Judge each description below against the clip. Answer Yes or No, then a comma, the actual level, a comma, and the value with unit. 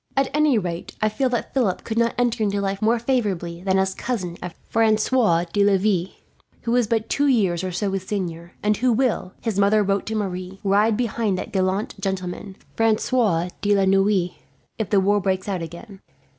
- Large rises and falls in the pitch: No, average, 3.2 semitones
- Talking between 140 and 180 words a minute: No, average, 195 wpm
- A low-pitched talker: No, high, 200 Hz